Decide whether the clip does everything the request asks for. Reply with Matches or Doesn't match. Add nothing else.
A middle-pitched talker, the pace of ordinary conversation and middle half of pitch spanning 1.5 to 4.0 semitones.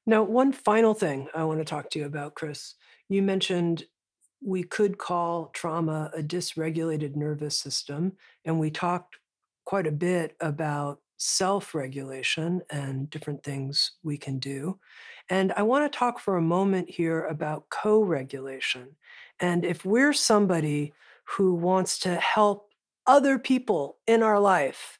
Doesn't match